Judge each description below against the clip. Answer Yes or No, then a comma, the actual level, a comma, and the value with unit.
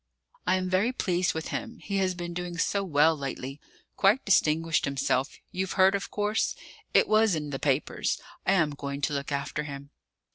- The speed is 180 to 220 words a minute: Yes, average, 185 wpm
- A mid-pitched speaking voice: Yes, medium, 170 Hz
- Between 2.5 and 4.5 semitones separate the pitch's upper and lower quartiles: No, average, 5.1 semitones